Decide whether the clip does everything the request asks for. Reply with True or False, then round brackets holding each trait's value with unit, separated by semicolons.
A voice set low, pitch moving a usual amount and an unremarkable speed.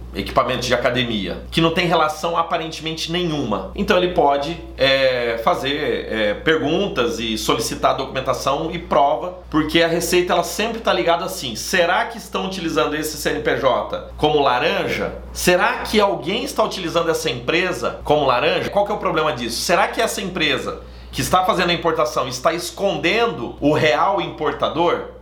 False (165 Hz; 3.5 semitones; 155 wpm)